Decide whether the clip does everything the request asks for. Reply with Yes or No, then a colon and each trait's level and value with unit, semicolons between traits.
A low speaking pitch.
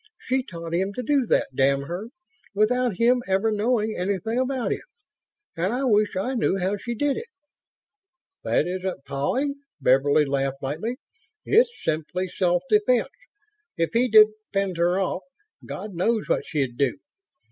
No: high, 200 Hz